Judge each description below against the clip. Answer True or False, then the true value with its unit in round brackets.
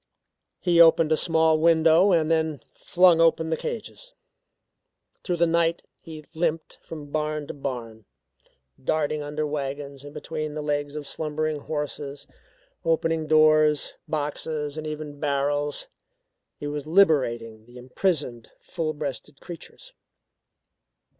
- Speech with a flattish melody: True (1.9 semitones)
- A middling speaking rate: False (125 wpm)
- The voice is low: False (155 Hz)